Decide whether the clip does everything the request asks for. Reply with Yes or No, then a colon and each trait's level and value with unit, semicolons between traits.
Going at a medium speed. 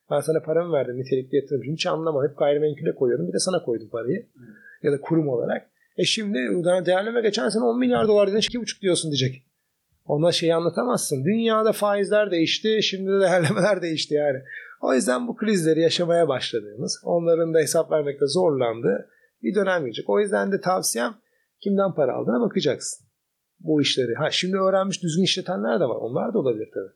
No: fast, 175 wpm